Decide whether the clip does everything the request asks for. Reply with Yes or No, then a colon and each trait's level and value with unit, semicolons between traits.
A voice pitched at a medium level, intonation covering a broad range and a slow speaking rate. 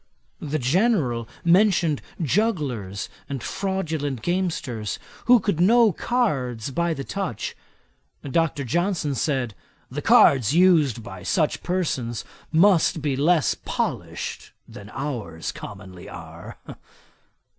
Yes: medium, 150 Hz; wide, 6.9 semitones; slow, 105 wpm